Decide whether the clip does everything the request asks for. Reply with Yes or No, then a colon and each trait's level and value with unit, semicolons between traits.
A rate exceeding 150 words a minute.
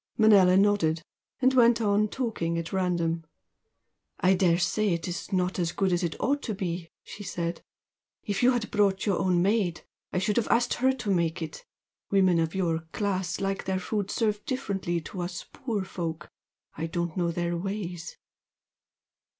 Yes: average, 170 wpm